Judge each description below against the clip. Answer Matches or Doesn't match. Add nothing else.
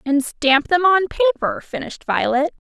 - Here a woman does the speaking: Matches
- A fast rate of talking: Doesn't match